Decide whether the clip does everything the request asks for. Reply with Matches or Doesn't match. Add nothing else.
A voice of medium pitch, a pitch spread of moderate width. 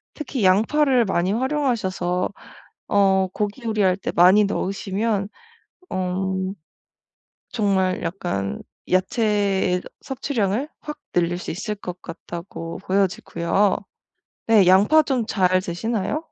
Doesn't match